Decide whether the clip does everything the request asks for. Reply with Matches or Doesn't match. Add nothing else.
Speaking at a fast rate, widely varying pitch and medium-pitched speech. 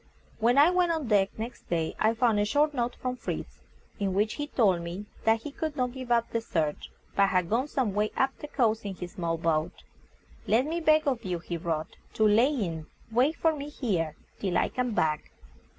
Doesn't match